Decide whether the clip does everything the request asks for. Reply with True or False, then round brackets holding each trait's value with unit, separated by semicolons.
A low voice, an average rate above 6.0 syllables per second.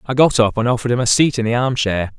True (120 Hz; 6.8 syllables/s)